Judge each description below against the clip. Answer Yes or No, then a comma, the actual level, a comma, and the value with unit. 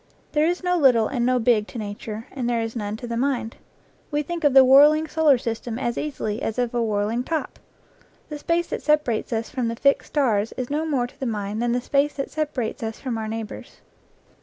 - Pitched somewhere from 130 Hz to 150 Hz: No, high, 245 Hz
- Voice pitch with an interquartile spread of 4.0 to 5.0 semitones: Yes, average, 4.4 semitones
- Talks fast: Yes, fast, 225 wpm